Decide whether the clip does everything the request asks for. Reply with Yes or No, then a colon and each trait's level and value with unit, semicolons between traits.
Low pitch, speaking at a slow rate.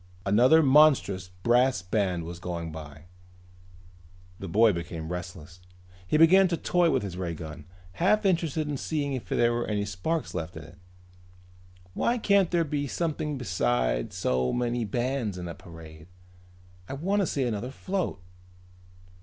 No: low, 115 Hz; average, 150 wpm